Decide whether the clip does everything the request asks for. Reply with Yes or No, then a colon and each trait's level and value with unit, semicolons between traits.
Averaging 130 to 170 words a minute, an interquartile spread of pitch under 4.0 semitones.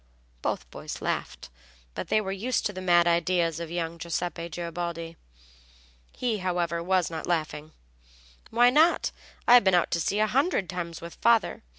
Yes: average, 160 wpm; average, 3.5 semitones